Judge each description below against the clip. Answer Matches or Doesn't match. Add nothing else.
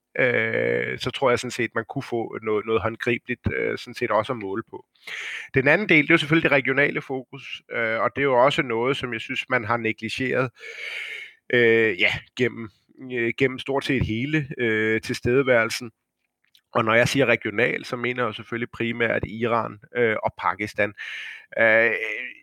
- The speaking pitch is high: Doesn't match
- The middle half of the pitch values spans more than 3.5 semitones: Matches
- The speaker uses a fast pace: Doesn't match